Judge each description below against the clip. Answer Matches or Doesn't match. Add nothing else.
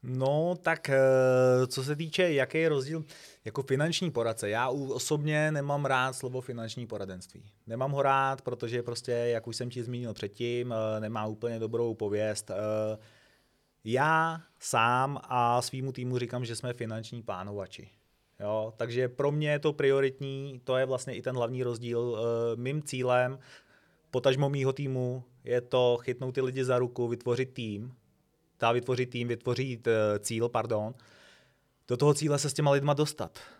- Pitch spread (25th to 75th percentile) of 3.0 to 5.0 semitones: Doesn't match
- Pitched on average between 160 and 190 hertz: Doesn't match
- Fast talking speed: Doesn't match